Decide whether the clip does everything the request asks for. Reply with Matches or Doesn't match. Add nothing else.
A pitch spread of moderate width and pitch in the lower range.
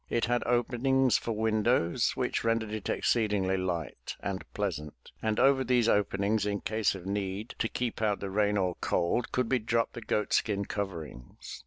Matches